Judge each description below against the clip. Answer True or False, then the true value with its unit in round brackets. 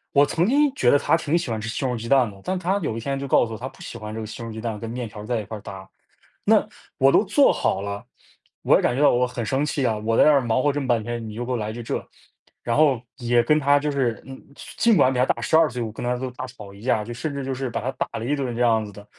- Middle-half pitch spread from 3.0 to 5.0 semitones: True (3.8 semitones)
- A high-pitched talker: False (125 Hz)